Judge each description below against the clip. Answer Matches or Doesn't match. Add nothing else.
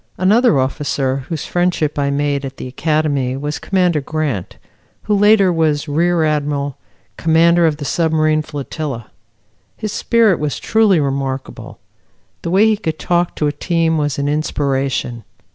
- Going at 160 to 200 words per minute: Doesn't match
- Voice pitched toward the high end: Doesn't match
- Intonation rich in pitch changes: Doesn't match